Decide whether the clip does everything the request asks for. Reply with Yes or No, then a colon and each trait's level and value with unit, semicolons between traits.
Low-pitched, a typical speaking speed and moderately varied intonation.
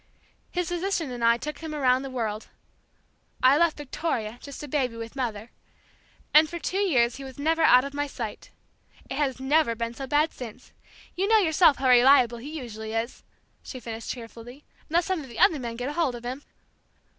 No: very high, 265 Hz; average, 195 wpm; average, 4.4 semitones